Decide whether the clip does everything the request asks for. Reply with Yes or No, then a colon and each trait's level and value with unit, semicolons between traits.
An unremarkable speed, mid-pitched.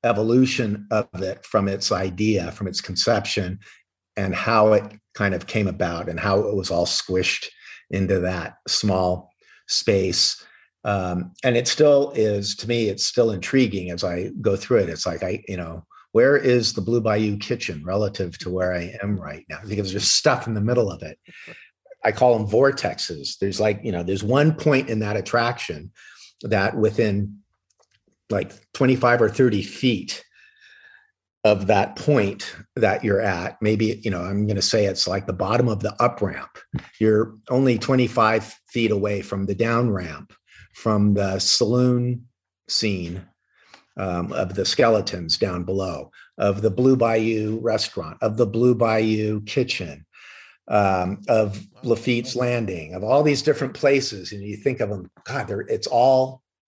No: average, 165 wpm; low, 105 Hz